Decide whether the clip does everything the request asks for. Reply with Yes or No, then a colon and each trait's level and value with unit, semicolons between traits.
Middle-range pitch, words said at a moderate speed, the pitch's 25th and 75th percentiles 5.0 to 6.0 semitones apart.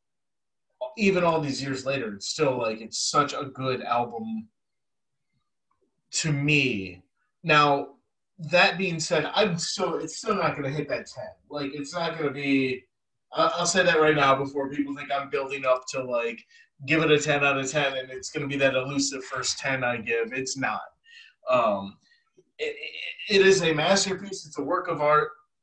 Yes: medium, 145 Hz; average, 180 wpm; wide, 5.5 semitones